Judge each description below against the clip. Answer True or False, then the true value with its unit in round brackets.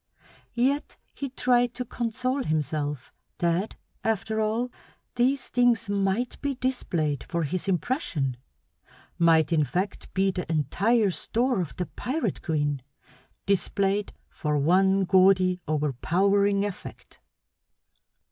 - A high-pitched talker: True (195 Hz)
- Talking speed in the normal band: False (110 wpm)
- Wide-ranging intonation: True (6.5 semitones)